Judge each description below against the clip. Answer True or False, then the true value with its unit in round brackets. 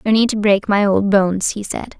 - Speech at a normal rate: False (270 wpm)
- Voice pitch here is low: False (205 Hz)